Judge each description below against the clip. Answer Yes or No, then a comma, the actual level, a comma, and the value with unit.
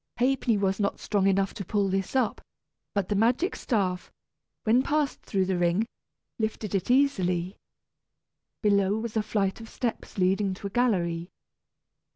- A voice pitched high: Yes, high, 200 Hz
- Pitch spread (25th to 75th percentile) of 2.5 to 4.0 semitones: Yes, average, 3.1 semitones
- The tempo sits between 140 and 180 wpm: Yes, average, 155 wpm